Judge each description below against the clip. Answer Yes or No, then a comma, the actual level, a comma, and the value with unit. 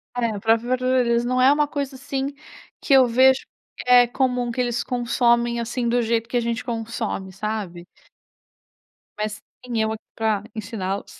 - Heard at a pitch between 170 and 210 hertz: No, high, 235 Hz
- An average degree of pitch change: No, narrow, 2.3 semitones